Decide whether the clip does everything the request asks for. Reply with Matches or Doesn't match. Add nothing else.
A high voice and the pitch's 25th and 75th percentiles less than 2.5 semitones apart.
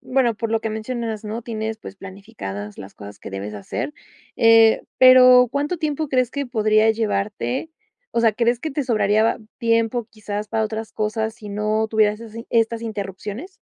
Matches